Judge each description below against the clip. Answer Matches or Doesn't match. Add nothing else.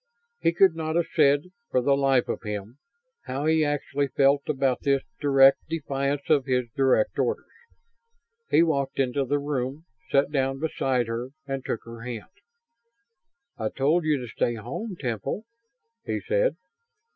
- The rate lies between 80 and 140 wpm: Doesn't match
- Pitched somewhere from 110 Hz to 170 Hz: Matches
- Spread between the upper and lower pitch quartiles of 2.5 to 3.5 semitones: Matches